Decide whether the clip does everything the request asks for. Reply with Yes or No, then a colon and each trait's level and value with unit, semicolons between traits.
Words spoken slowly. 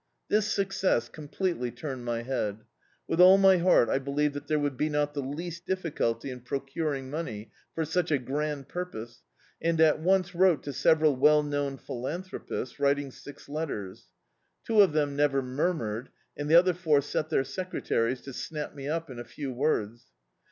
No: average, 180 wpm